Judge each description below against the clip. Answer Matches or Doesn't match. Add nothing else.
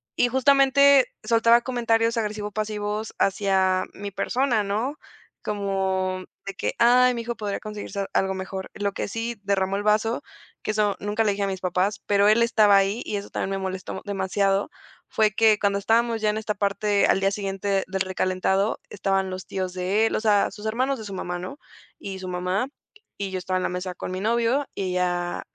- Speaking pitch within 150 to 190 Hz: Doesn't match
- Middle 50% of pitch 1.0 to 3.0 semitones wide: Matches